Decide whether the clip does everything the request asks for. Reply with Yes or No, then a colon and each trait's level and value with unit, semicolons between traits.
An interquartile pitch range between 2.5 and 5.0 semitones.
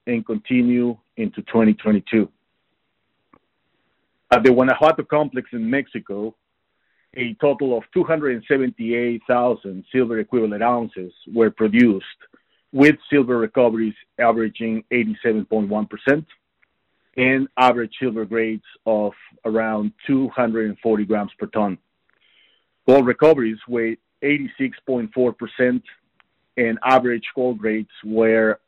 Yes: average, 2.8 semitones